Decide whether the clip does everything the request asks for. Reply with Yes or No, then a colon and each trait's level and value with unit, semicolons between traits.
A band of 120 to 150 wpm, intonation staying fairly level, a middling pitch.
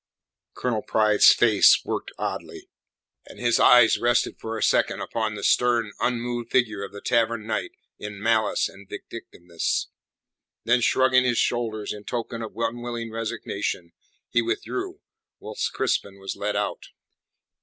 No: average, 140 wpm; narrow, 2.3 semitones; low, 115 Hz